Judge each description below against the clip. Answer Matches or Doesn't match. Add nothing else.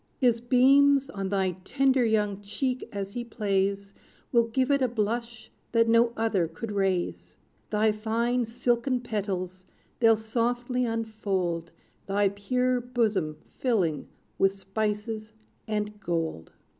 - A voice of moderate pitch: Doesn't match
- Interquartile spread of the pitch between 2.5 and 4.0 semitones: Matches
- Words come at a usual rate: Doesn't match